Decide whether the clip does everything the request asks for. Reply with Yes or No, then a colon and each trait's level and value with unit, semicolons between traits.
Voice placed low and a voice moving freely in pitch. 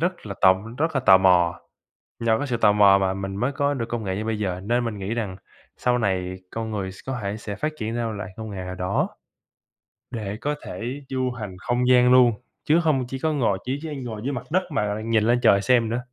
No: low, 115 Hz; average, 4.3 semitones